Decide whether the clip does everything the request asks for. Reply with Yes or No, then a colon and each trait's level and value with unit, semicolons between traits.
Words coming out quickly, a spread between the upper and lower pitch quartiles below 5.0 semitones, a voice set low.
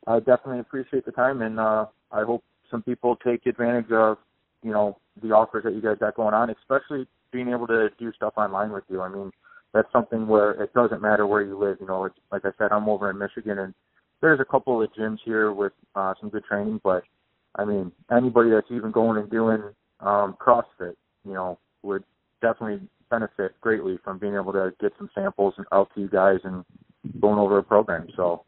Yes: fast, 210 wpm; average, 2.9 semitones; low, 105 Hz